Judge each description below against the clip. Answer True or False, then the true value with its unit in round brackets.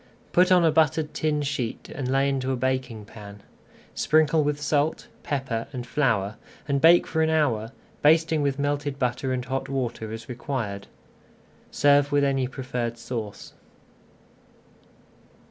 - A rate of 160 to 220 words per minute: False (145 wpm)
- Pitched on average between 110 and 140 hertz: True (135 Hz)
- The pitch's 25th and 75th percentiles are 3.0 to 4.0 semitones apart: True (3.4 semitones)